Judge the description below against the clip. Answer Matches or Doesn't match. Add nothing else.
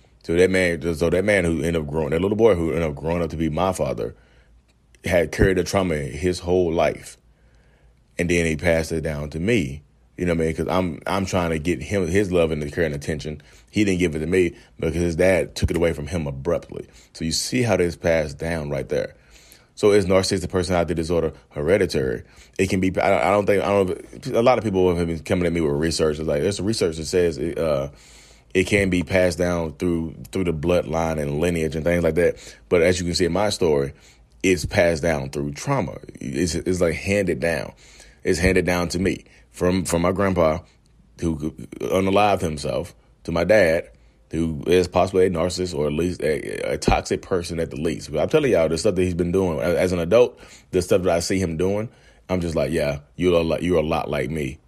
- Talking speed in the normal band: Doesn't match